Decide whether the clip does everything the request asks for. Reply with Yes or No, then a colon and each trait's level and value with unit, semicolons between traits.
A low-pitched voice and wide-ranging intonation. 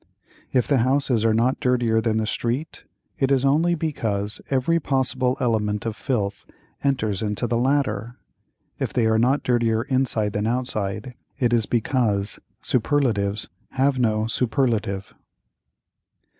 No: low, 120 Hz; average, 3.4 semitones